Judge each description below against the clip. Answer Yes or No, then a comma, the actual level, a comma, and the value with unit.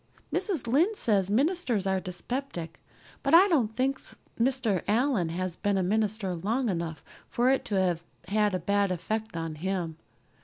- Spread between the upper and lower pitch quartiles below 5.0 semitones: No, wide, 5.6 semitones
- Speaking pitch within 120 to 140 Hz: No, high, 205 Hz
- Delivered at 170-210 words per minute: No, average, 160 wpm